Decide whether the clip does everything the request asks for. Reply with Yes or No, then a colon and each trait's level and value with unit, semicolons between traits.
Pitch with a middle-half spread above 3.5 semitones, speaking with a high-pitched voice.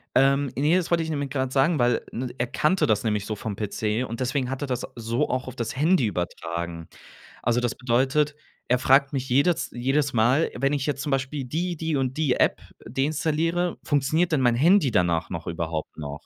No: average, 4.1 semitones; low, 130 Hz